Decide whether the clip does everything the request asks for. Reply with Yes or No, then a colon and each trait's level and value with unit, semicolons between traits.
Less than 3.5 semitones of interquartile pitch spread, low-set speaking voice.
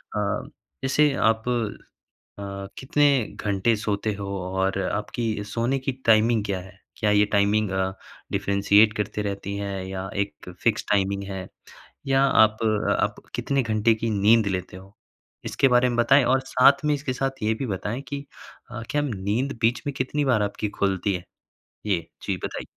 No: average, 3.8 semitones; low, 110 Hz